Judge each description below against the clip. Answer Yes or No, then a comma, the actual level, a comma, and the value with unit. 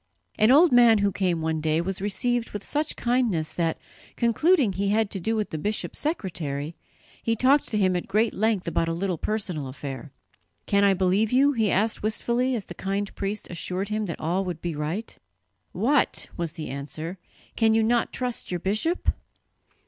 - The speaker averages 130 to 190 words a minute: Yes, average, 185 wpm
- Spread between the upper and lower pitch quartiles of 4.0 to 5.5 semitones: Yes, average, 4.9 semitones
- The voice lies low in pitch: No, high, 200 Hz